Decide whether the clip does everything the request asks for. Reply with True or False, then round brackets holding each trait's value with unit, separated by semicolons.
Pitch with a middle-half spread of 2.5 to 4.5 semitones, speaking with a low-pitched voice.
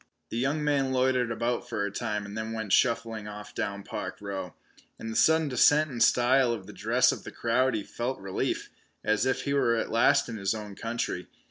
True (3.6 semitones; 115 Hz)